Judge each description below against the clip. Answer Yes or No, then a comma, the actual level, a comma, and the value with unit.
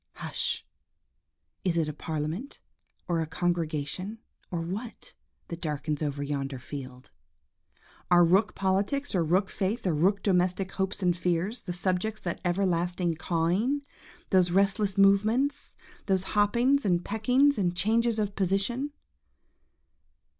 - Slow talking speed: Yes, slow, 130 wpm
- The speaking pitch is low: No, medium, 185 Hz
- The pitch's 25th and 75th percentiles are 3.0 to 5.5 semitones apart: Yes, average, 3.6 semitones